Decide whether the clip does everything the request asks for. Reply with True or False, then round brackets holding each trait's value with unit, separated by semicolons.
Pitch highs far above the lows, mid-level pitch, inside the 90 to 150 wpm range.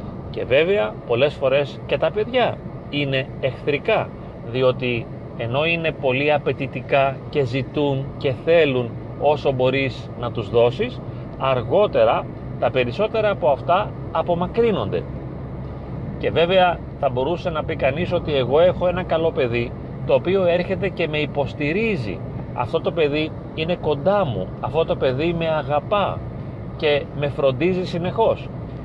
False (4.6 semitones; 145 Hz; 130 wpm)